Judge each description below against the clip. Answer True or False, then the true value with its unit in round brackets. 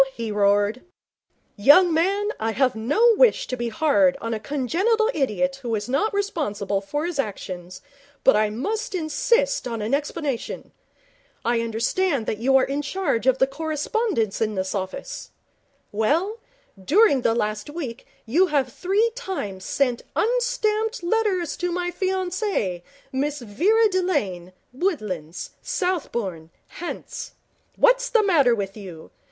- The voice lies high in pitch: True (280 Hz)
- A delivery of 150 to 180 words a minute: False (140 wpm)